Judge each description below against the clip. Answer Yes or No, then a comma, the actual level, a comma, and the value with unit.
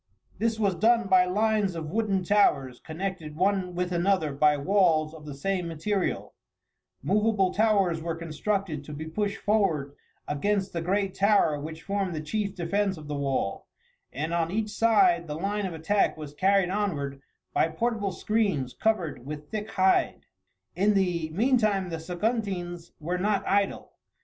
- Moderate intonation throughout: Yes, average, 4.5 semitones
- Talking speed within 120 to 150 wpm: No, average, 160 wpm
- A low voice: No, medium, 185 Hz